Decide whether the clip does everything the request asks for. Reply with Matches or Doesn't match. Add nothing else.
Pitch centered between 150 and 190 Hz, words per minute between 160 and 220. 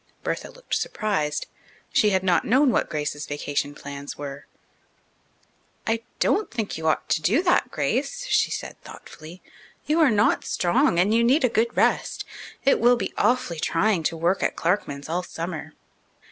Matches